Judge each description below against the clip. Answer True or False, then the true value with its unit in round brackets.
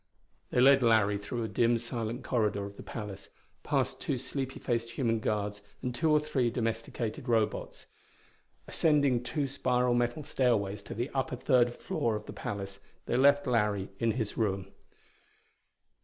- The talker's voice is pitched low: True (120 Hz)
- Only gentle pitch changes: False (3.2 semitones)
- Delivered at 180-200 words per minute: False (155 wpm)